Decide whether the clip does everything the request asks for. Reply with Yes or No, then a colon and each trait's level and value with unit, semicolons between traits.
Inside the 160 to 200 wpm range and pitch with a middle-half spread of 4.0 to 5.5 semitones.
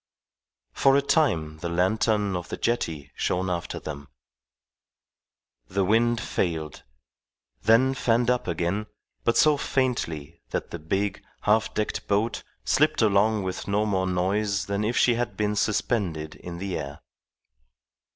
No: average, 140 wpm; average, 4.8 semitones